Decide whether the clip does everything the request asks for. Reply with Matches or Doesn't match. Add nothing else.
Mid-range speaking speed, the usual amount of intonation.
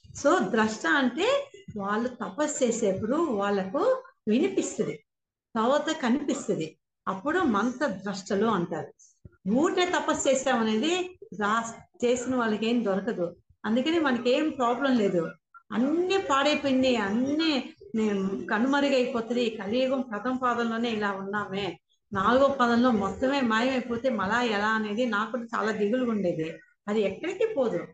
Matches